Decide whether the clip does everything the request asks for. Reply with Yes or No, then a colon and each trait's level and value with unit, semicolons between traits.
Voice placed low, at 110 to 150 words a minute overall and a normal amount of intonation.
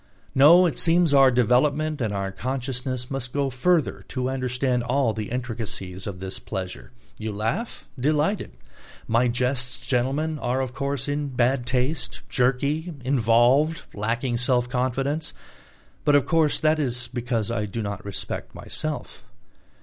Yes: low, 125 Hz; average, 140 wpm; average, 3.1 semitones